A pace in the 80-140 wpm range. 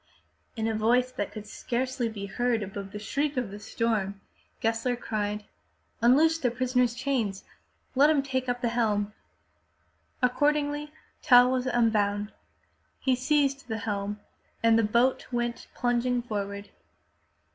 Yes: slow, 135 wpm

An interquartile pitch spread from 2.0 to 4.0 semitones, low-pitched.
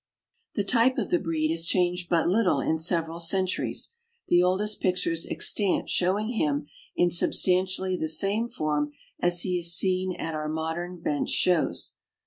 No: narrow, 2.4 semitones; medium, 175 Hz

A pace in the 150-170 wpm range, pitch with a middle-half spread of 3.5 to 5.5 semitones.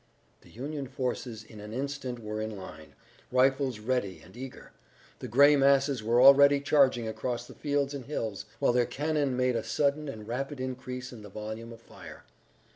No: average, 180 wpm; average, 3.8 semitones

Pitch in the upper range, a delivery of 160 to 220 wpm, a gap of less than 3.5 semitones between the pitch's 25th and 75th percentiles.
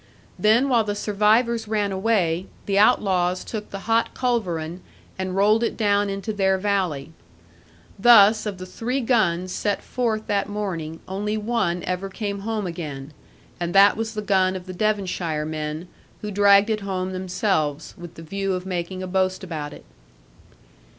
Yes: high, 195 Hz; average, 165 wpm; average, 2.9 semitones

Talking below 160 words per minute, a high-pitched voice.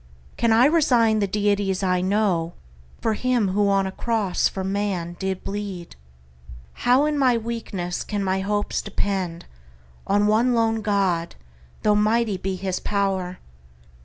Yes: average, 145 wpm; high, 205 Hz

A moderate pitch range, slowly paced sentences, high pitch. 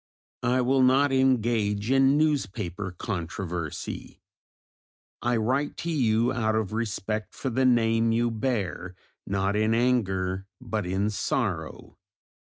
No: average, 4.0 semitones; slow, 120 wpm; low, 115 Hz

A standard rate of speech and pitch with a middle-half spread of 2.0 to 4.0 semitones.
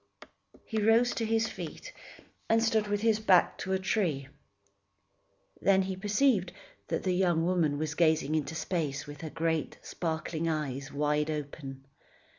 No: average, 150 wpm; wide, 5.4 semitones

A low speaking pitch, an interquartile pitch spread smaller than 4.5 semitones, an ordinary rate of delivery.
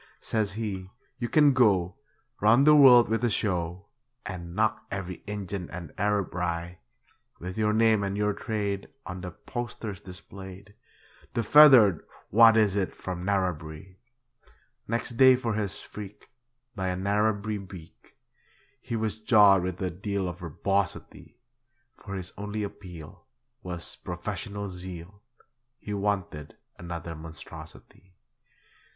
No: low, 100 Hz; average, 3.0 semitones; slow, 130 wpm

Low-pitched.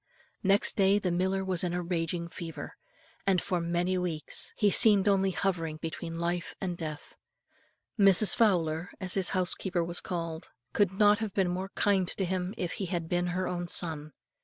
No: medium, 180 Hz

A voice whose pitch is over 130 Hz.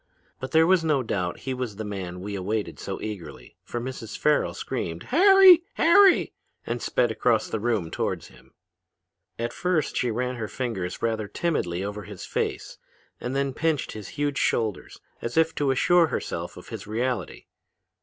No: low, 120 Hz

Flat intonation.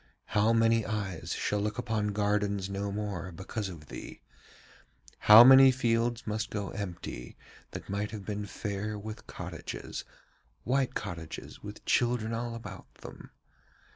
Yes: narrow, 2.2 semitones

